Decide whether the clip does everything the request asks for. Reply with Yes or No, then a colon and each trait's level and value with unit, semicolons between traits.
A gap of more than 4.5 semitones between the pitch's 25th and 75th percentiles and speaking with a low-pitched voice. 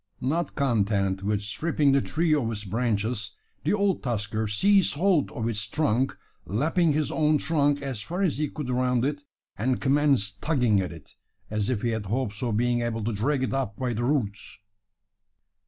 Yes: wide, 5.6 semitones; low, 125 Hz